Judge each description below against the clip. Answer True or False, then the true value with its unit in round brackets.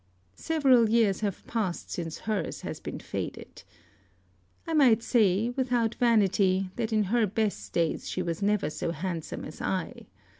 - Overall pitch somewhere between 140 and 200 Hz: False (215 Hz)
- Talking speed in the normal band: True (150 wpm)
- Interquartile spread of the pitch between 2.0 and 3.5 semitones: False (4.1 semitones)